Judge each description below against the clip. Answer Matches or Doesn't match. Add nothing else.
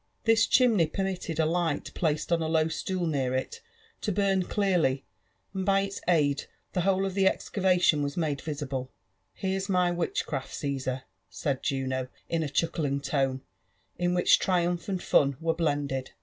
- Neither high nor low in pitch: Matches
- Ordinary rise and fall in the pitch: Matches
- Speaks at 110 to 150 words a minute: Doesn't match